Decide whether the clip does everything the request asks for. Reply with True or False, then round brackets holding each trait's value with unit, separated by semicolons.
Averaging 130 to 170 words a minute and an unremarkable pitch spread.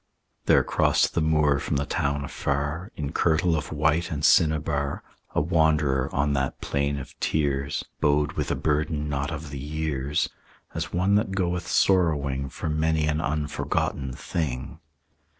False (150 wpm; 2.0 semitones)